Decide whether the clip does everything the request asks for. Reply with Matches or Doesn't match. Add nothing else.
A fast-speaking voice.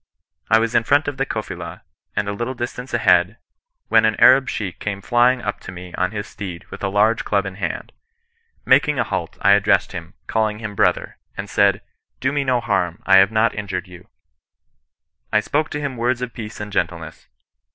Matches